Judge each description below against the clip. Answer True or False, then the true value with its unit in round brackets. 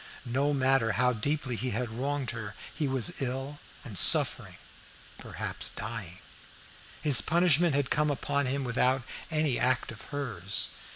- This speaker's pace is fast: False (140 wpm)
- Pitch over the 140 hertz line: False (130 Hz)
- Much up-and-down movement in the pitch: False (3.6 semitones)